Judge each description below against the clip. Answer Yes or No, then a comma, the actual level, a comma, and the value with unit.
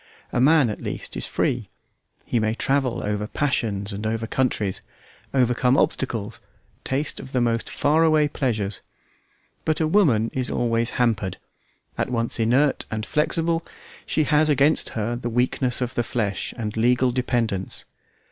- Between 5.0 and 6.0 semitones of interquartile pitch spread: No, average, 3.7 semitones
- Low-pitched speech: Yes, low, 120 Hz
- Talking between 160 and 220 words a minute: No, average, 150 wpm